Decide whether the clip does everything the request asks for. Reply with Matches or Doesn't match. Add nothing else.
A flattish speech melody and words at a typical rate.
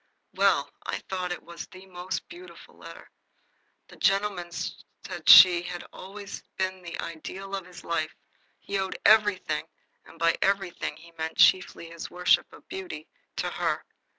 Matches